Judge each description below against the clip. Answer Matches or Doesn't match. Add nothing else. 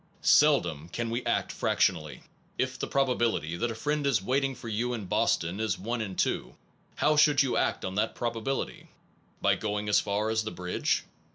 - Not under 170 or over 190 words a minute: Matches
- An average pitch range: Matches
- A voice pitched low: Matches